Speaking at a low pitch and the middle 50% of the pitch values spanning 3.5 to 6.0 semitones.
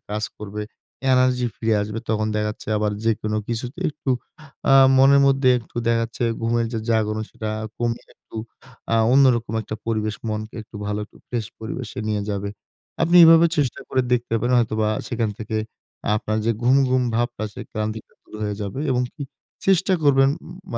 No: low, 115 Hz; average, 3.0 semitones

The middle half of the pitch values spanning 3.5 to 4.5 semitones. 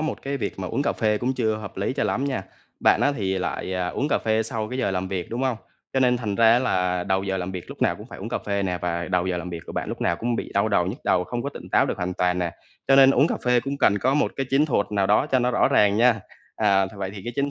No: average, 5.3 semitones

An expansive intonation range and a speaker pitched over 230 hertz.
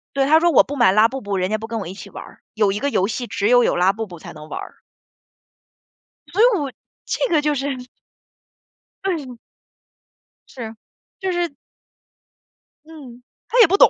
Yes: wide, 6.5 semitones; very high, 250 Hz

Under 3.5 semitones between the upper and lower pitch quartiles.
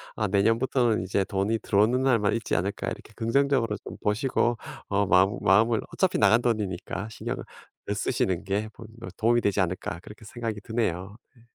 Yes: average, 2.8 semitones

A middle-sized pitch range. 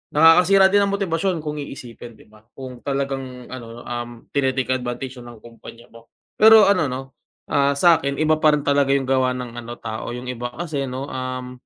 Yes: average, 3.6 semitones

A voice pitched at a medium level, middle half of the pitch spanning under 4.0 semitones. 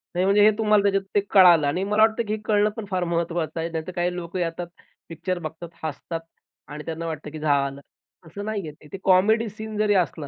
No: medium, 175 Hz; average, 4.3 semitones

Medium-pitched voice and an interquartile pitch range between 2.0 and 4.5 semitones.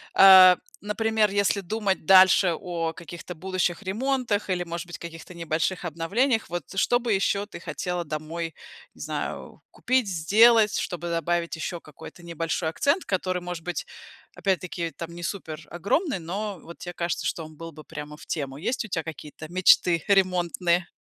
Yes: medium, 175 Hz; average, 3.1 semitones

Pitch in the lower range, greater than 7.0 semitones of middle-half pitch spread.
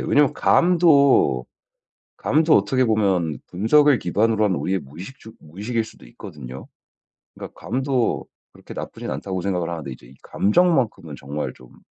Yes: low, 105 Hz; wide, 8.4 semitones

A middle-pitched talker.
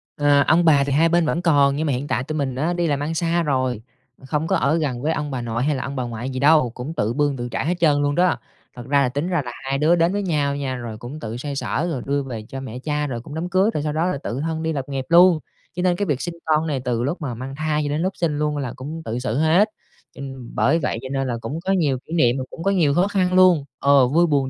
Yes: medium, 145 Hz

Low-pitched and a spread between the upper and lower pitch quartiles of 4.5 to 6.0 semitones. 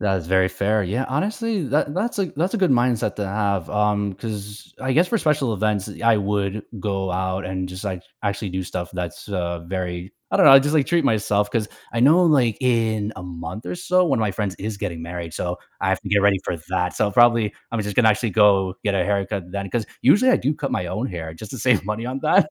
Yes: low, 105 Hz; average, 4.8 semitones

